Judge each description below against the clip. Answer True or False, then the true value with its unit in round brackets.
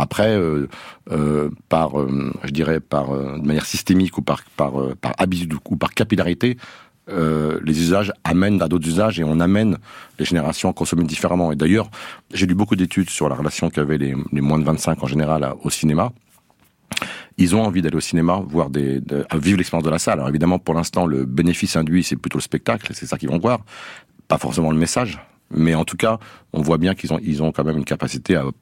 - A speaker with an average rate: False (225 wpm)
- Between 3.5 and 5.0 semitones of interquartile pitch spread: False (3.0 semitones)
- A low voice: True (80 Hz)